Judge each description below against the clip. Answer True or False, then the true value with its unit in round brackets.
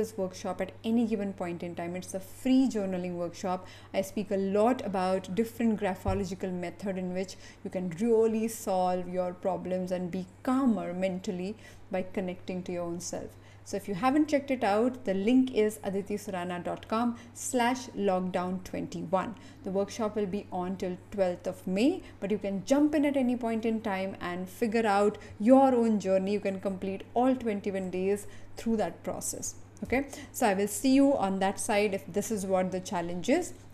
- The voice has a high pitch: True (200 Hz)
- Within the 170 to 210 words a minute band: True (180 wpm)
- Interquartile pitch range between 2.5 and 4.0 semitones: True (3.5 semitones)